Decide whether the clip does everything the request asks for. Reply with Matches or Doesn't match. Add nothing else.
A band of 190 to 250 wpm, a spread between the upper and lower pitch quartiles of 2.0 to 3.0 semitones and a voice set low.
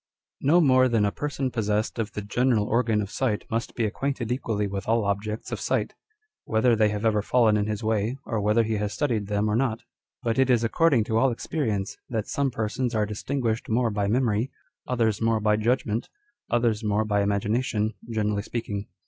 Matches